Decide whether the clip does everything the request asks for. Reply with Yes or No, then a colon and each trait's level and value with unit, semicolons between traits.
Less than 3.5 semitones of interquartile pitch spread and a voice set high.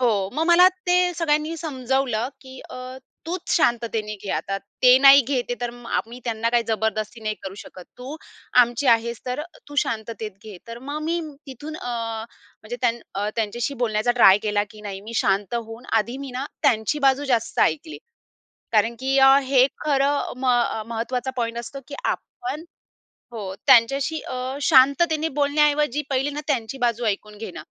No: average, 3.9 semitones; high, 245 Hz